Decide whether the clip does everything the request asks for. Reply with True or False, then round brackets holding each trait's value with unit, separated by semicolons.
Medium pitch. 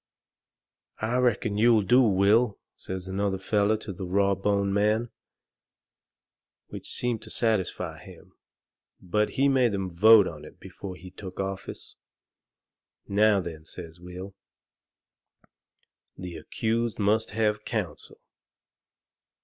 False (100 Hz)